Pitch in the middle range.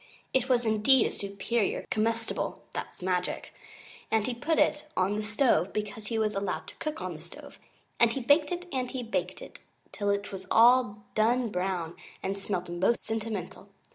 No: high, 215 Hz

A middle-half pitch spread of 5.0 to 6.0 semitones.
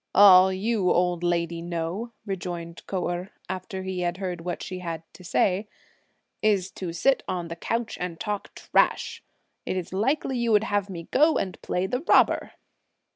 No: average, 2.8 semitones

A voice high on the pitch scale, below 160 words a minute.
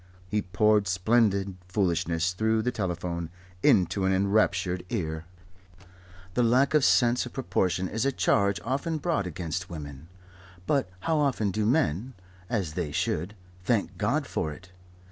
No: low, 100 Hz; average, 145 wpm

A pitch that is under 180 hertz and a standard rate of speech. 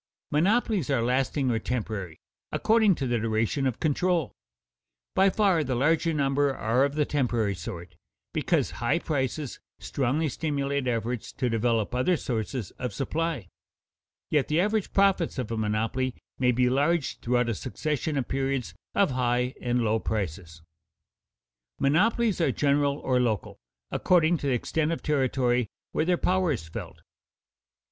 Yes: low, 135 Hz; average, 150 wpm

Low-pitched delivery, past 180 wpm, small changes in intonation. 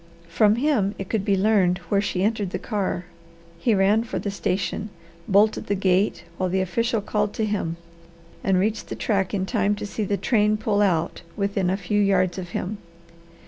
No: high, 200 Hz; average, 190 wpm; narrow, 2.0 semitones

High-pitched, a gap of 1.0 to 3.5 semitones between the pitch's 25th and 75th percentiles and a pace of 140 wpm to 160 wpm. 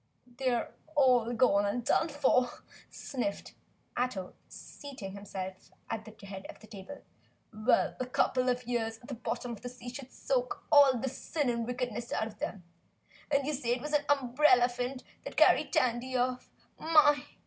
No: high, 245 Hz; average, 3.0 semitones; average, 175 wpm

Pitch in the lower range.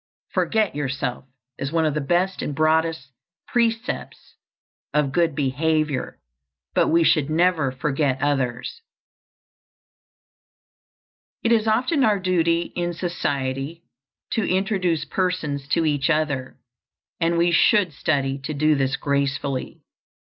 No: medium, 155 Hz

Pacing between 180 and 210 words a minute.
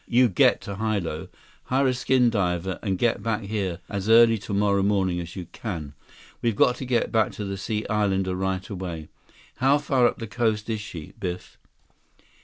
Yes: average, 185 wpm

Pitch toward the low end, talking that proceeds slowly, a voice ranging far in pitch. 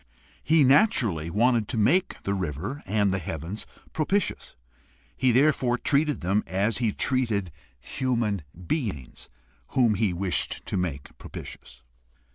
Yes: low, 105 Hz; slow, 125 wpm; wide, 5.8 semitones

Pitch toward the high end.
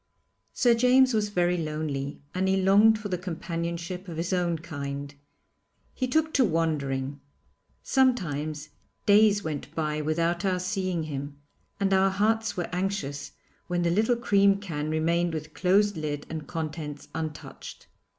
No: medium, 175 Hz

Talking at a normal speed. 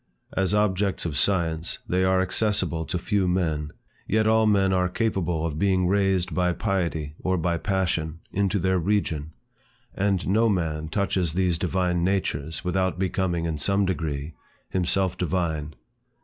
Yes: average, 150 wpm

